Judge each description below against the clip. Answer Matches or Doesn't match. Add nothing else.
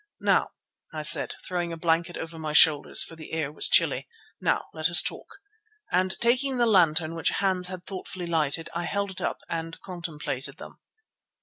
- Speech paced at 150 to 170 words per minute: Doesn't match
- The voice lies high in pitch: Doesn't match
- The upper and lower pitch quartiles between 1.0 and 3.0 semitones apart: Matches